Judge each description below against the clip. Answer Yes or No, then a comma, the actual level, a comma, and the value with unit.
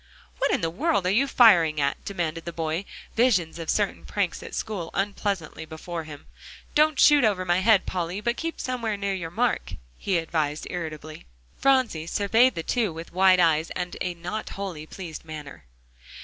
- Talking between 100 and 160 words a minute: No, average, 175 wpm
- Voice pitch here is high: No, medium, 180 Hz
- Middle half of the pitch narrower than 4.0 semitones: No, average, 4.6 semitones